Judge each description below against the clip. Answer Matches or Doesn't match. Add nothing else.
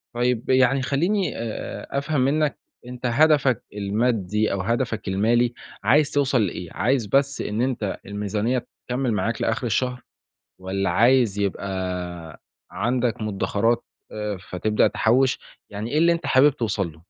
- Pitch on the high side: Doesn't match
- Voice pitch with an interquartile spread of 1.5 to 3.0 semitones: Doesn't match